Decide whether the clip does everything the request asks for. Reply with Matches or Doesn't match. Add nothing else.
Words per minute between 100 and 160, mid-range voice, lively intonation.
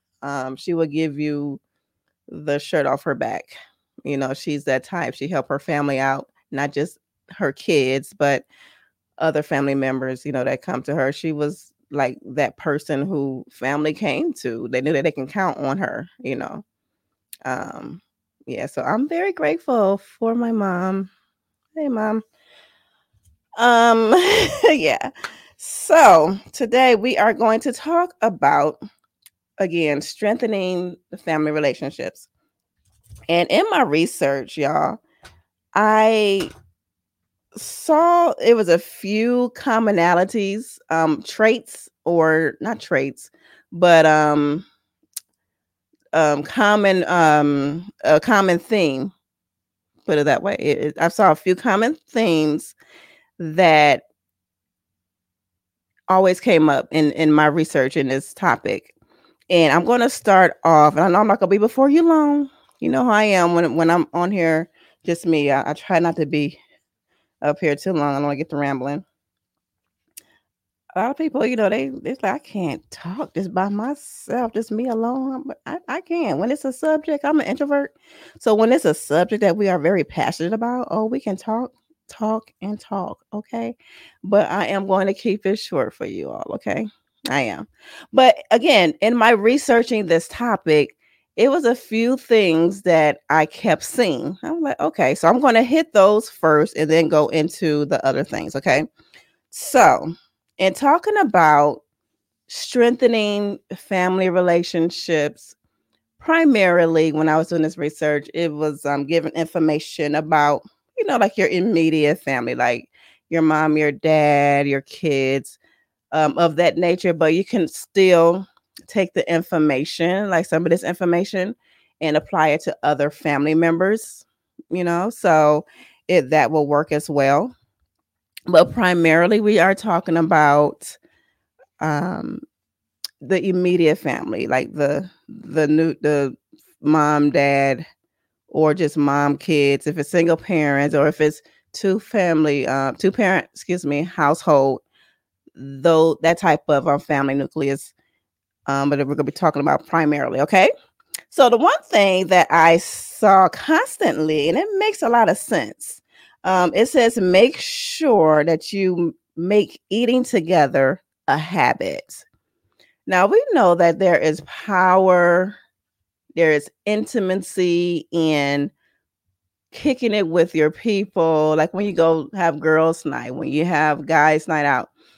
Matches